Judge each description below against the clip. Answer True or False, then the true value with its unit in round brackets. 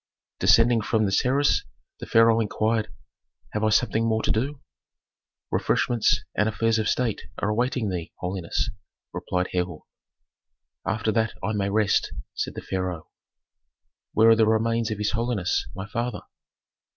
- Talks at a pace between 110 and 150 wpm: True (145 wpm)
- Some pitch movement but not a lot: False (2.3 semitones)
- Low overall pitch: True (110 Hz)